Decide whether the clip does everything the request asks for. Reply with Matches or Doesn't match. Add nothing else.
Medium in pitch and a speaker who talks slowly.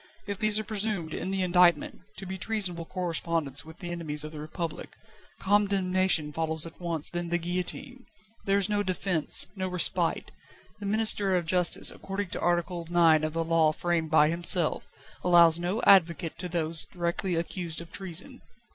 Doesn't match